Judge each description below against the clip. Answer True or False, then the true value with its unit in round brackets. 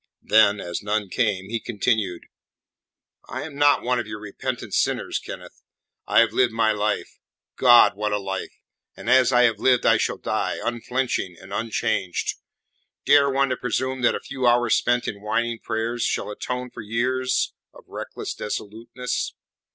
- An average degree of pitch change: True (3.2 semitones)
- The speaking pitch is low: True (115 Hz)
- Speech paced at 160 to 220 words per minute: True (165 wpm)